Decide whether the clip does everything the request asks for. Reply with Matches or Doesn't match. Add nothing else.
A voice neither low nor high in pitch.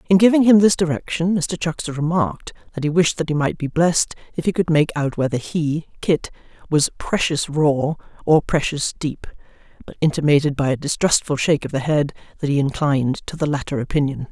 Matches